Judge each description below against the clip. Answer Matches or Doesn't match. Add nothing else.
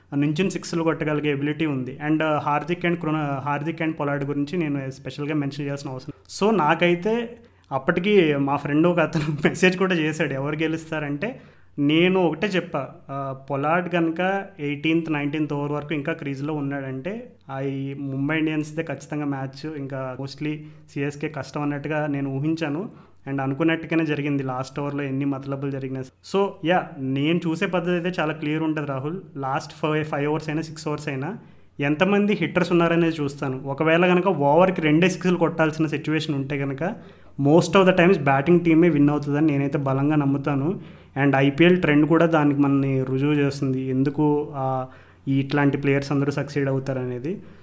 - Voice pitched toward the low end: Doesn't match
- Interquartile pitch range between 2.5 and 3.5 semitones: Matches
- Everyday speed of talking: Doesn't match